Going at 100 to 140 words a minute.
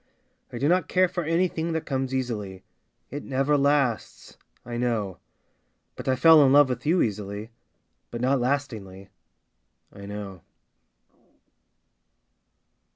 Yes: slow, 135 wpm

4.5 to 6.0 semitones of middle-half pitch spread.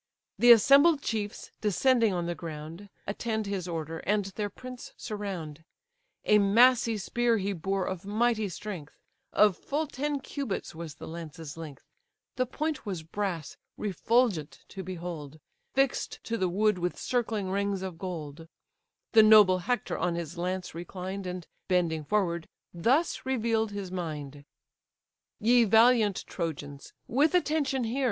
Yes: average, 5.2 semitones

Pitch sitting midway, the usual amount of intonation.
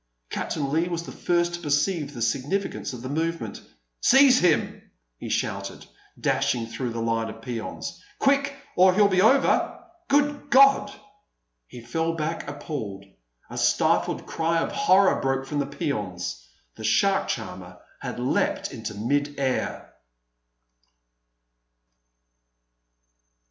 No: medium, 150 Hz; wide, 7.6 semitones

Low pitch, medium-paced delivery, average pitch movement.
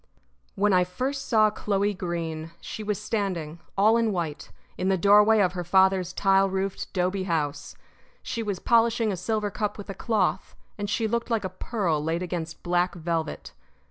No: high, 195 Hz; average, 175 wpm; average, 3.3 semitones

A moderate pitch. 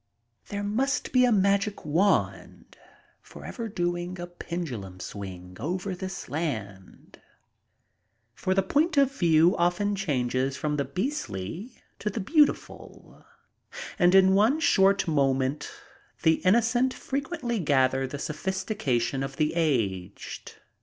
Yes: medium, 175 Hz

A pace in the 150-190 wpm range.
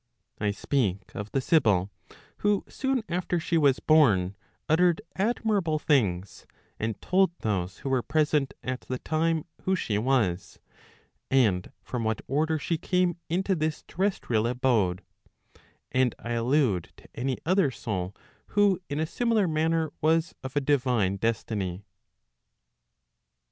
No: average, 140 wpm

